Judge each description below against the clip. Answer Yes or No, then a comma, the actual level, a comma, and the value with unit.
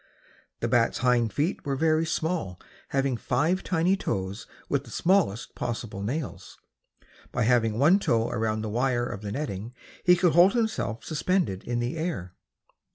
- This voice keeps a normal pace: Yes, average, 160 wpm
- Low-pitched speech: Yes, low, 125 Hz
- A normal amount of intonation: No, wide, 6.6 semitones